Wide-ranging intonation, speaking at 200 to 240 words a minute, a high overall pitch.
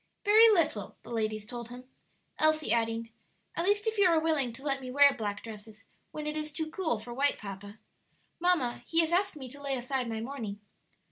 Yes: wide, 5.7 semitones; fast, 205 wpm; very high, 270 Hz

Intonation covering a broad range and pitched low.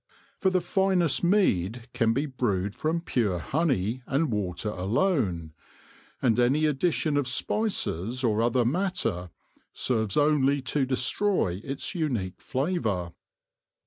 Yes: wide, 7.1 semitones; low, 130 Hz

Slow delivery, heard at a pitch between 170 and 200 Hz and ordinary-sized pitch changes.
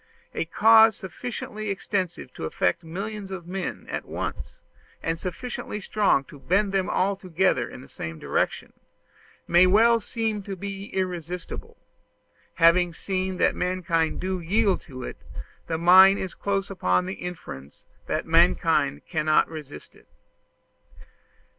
Yes: slow, 130 wpm; medium, 185 Hz; average, 3.3 semitones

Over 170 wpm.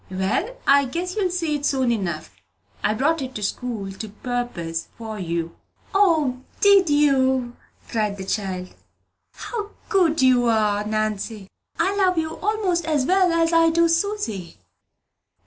No: average, 145 wpm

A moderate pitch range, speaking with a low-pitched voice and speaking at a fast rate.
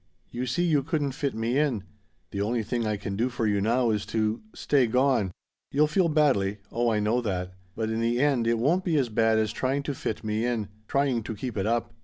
Yes: average, 4.1 semitones; low, 120 Hz; fast, 235 wpm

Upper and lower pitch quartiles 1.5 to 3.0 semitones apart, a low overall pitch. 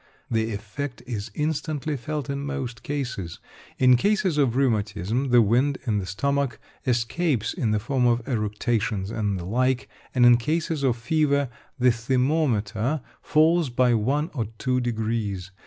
No: average, 4.2 semitones; low, 125 Hz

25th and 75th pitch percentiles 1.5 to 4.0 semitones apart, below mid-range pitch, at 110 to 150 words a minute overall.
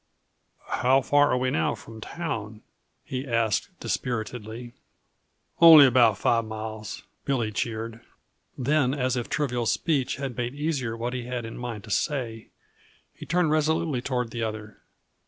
Yes: average, 3.3 semitones; low, 120 Hz; average, 145 wpm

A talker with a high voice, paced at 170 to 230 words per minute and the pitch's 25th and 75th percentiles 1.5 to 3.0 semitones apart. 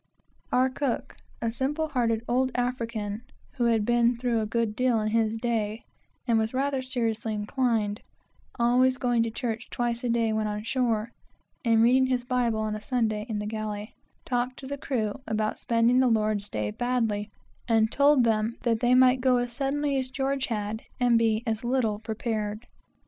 Yes: high, 235 Hz; average, 175 wpm; narrow, 2.5 semitones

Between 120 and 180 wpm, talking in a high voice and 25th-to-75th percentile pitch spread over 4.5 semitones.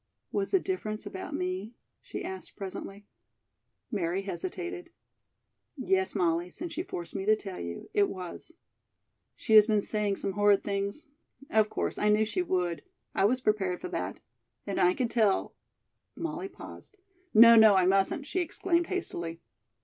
Yes: average, 160 wpm; high, 205 Hz; average, 5.2 semitones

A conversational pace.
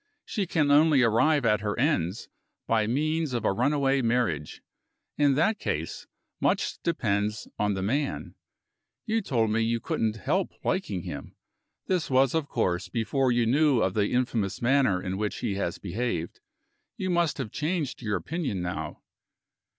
Yes: average, 160 wpm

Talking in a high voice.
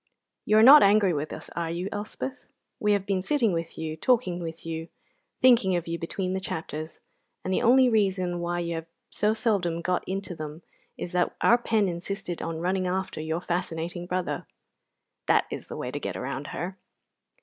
No: medium, 180 Hz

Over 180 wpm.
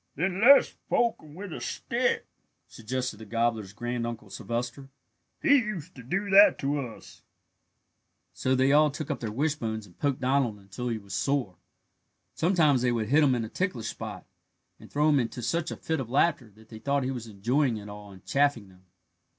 Yes: average, 190 wpm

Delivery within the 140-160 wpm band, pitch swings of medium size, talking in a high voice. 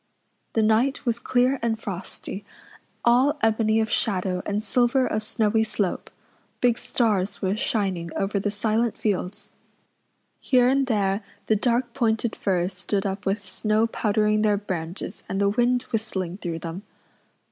Yes: average, 145 wpm; average, 3.1 semitones; high, 215 Hz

